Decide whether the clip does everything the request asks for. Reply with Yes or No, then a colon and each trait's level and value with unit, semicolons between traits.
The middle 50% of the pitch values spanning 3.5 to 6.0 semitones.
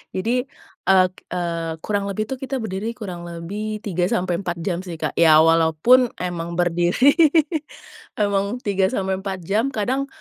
Yes: average, 3.8 semitones